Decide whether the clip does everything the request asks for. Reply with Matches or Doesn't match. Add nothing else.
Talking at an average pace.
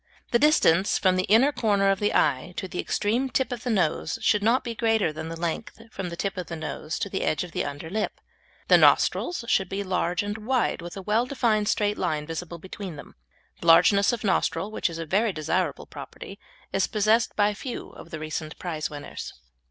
Doesn't match